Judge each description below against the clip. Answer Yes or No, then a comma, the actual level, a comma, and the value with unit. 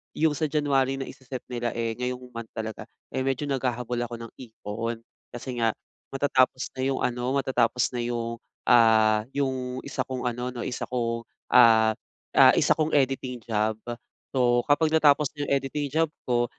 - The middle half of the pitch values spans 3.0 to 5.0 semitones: No, narrow, 2.4 semitones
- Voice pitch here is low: Yes, low, 125 Hz